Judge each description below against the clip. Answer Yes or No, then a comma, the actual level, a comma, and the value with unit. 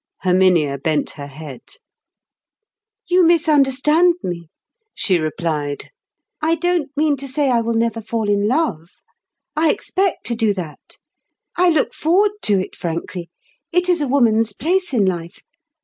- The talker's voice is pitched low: No, high, 230 Hz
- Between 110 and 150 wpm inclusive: Yes, average, 140 wpm